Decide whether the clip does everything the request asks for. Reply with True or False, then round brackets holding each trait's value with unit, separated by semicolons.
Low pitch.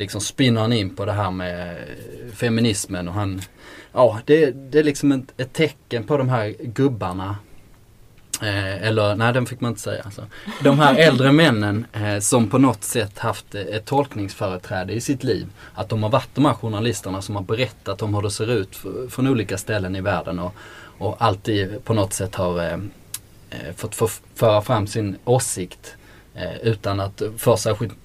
True (110 Hz)